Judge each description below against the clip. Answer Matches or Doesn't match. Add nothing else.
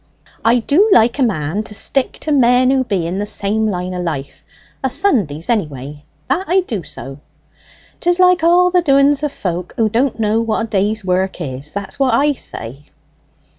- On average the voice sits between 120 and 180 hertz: Doesn't match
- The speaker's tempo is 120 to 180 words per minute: Doesn't match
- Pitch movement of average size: Doesn't match